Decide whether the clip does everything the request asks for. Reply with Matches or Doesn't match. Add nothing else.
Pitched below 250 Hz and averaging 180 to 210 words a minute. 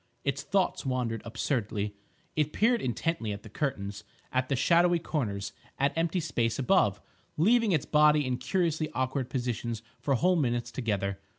Doesn't match